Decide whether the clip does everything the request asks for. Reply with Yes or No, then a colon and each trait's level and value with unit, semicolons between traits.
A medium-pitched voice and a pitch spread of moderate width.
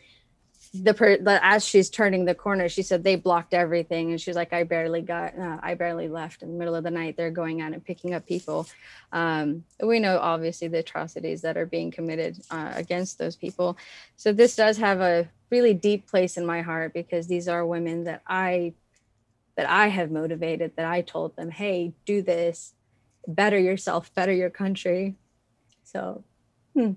No: medium, 175 Hz; narrow, 2.3 semitones